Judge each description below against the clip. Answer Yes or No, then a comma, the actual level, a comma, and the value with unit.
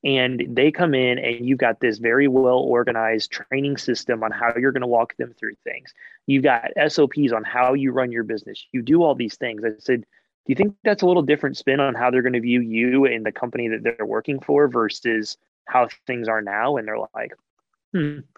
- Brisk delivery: Yes, fast, 225 wpm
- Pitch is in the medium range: No, low, 125 Hz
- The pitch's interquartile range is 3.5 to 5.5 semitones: No, average, 3.1 semitones